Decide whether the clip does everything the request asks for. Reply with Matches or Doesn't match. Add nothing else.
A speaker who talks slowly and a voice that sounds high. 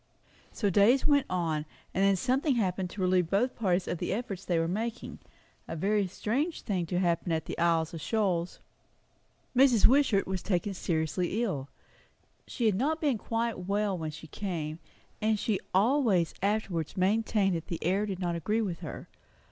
Doesn't match